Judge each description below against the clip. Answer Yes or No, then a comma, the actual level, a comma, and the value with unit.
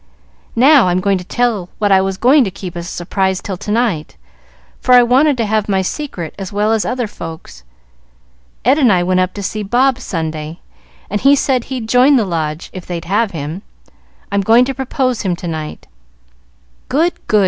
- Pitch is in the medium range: No, high, 205 Hz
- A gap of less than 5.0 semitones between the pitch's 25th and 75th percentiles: No, wide, 5.5 semitones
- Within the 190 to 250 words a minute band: Yes, average, 195 wpm